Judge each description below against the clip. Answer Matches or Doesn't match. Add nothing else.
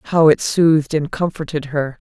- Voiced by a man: Doesn't match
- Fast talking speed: Doesn't match